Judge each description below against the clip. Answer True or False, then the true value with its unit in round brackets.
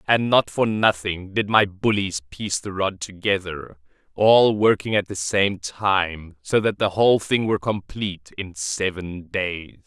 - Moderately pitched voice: False (95 Hz)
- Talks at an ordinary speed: True (165 wpm)